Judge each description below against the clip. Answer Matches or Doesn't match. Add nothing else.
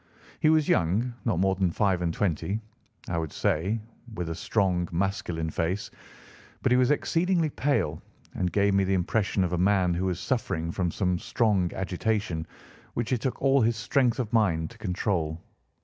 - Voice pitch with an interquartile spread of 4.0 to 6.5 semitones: Matches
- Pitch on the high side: Doesn't match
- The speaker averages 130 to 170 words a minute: Doesn't match